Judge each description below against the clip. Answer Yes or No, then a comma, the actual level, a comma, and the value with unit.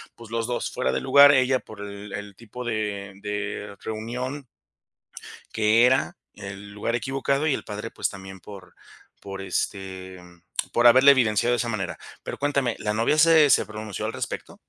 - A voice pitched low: Yes, low, 110 Hz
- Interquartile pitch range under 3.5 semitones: No, average, 3.9 semitones